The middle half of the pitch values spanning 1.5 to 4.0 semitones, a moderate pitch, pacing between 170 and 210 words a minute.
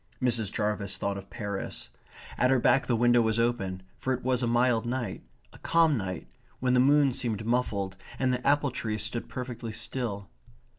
No: average, 3.1 semitones; low, 120 Hz; average, 185 wpm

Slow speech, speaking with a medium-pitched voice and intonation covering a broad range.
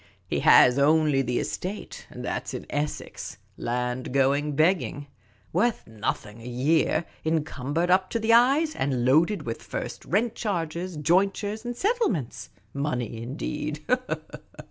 Yes: slow, 130 wpm; medium, 155 Hz; wide, 6.4 semitones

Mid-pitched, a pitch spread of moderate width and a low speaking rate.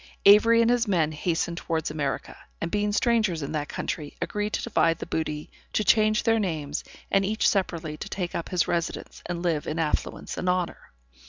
No: medium, 175 Hz; average, 4.7 semitones; average, 190 wpm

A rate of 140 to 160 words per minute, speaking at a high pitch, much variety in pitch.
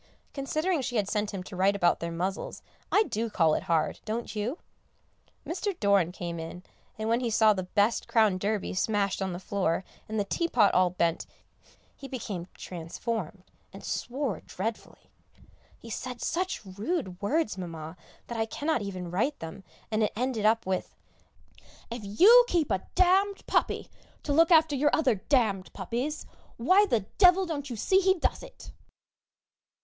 No: average, 175 wpm; high, 215 Hz; wide, 6.7 semitones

